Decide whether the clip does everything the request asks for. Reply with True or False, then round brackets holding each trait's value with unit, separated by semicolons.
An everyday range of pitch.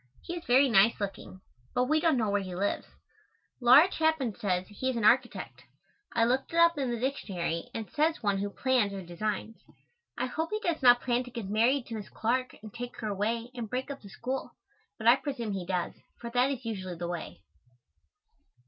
True (4.4 semitones)